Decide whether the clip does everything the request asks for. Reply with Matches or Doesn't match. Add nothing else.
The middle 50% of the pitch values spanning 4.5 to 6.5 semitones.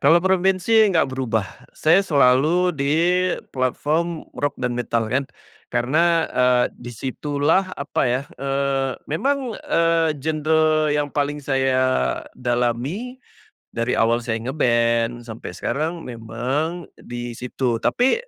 Matches